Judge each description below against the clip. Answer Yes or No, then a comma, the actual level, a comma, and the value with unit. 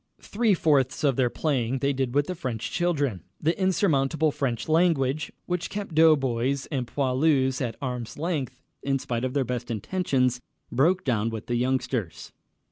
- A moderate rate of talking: Yes, average, 160 wpm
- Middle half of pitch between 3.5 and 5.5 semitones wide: Yes, average, 4.1 semitones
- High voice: No, low, 135 Hz